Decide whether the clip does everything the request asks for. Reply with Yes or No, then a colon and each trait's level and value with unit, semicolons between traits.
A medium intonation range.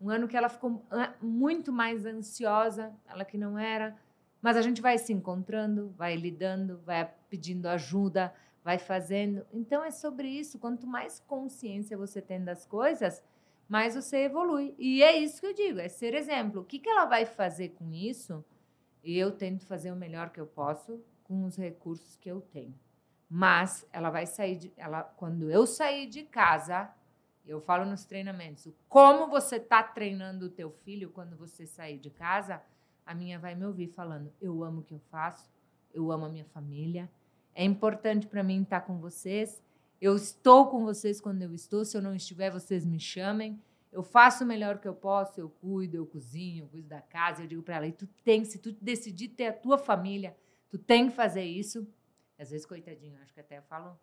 Yes: average, 4.7 semitones